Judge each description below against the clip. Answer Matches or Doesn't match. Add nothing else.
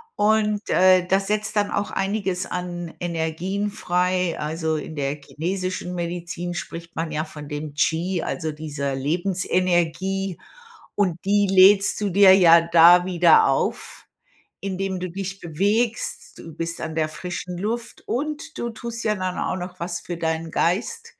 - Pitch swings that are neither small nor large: Matches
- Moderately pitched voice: Matches